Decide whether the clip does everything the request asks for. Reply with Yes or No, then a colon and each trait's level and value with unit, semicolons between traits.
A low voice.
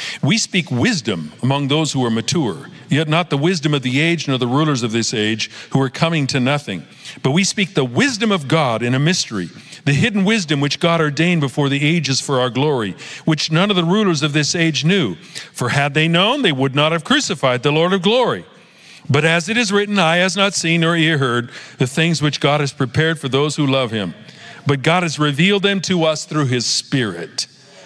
No: medium, 155 Hz